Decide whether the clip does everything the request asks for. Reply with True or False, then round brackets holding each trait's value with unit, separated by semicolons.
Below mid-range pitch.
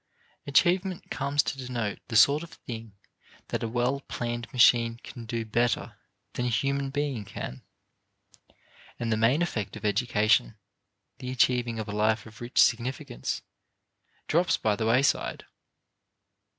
True (120 Hz)